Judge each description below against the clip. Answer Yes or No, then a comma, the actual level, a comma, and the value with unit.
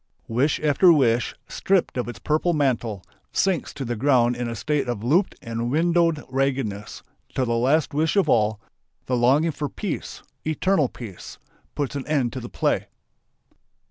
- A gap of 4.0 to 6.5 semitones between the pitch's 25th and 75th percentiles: Yes, average, 4.5 semitones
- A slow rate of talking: No, average, 165 wpm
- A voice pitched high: No, low, 135 Hz